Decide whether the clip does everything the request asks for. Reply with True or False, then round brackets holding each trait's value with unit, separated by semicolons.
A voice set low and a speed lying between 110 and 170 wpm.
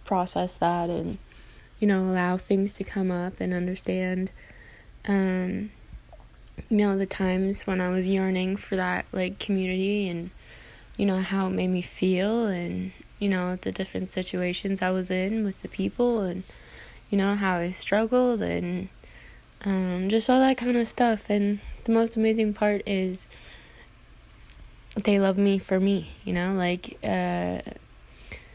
False (190 Hz; 155 wpm)